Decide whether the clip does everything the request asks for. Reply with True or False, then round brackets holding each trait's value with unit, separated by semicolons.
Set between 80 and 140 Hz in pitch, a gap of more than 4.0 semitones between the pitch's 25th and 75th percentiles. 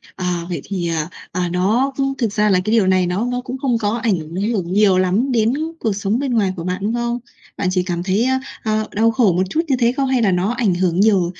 False (205 Hz; 4.4 semitones)